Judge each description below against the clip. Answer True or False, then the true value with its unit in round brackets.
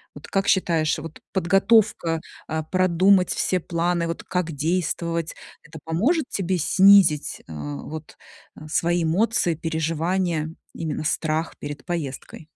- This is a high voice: False (170 Hz)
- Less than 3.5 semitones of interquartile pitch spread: True (2.7 semitones)